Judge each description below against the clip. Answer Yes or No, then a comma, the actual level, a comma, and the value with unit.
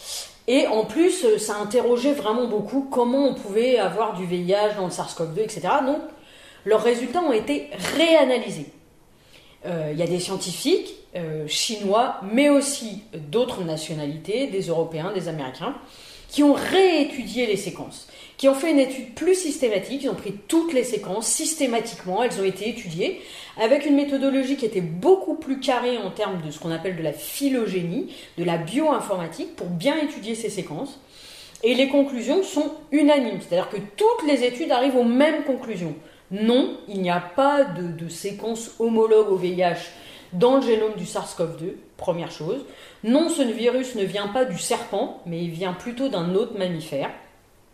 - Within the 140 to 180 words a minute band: Yes, average, 170 wpm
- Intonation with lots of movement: Yes, wide, 7.0 semitones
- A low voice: No, high, 225 Hz